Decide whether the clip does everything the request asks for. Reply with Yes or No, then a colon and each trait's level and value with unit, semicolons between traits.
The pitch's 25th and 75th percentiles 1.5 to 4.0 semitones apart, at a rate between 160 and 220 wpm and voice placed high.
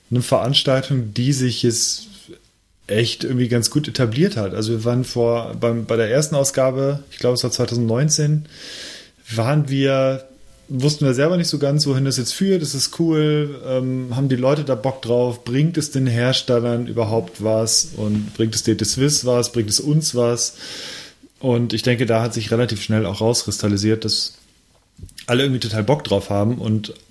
No: average, 3.2 semitones; average, 180 wpm; low, 125 Hz